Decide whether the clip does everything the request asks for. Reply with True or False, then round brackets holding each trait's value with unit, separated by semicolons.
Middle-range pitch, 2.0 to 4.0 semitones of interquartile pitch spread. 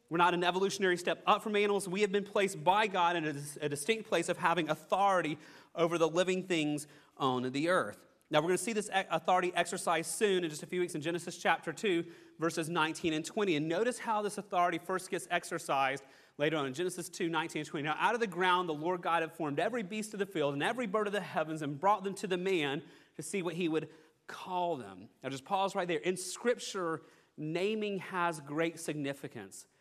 True (175 Hz; 3.4 semitones)